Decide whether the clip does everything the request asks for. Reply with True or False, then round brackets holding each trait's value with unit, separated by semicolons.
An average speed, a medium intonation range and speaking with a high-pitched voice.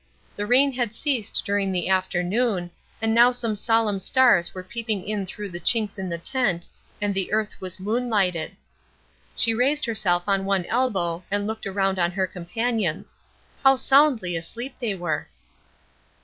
True (165 wpm; 4.0 semitones; 205 Hz)